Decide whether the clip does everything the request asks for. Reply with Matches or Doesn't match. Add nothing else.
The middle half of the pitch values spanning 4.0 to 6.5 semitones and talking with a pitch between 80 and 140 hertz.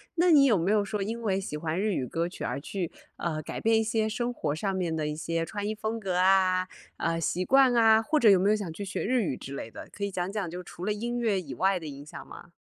Doesn't match